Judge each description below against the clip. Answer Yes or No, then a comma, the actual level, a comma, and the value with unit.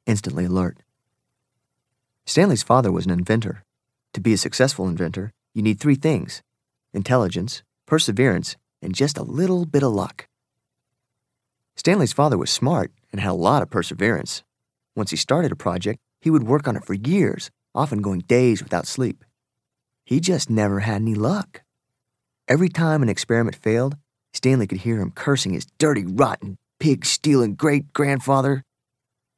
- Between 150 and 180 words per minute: Yes, average, 155 wpm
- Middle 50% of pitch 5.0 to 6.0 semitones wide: Yes, wide, 5.5 semitones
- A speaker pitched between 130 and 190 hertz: No, low, 120 Hz